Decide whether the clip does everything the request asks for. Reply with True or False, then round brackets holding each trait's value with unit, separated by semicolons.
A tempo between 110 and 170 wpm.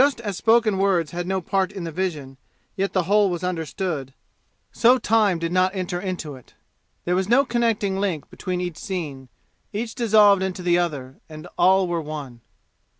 False (180 wpm)